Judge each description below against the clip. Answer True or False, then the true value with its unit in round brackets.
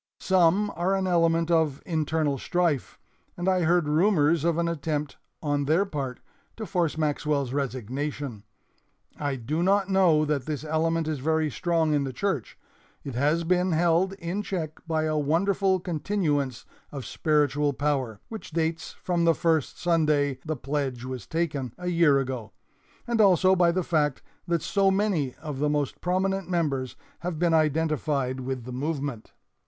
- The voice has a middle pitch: True (155 Hz)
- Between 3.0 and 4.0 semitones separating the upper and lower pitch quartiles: True (3.5 semitones)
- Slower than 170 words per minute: True (160 wpm)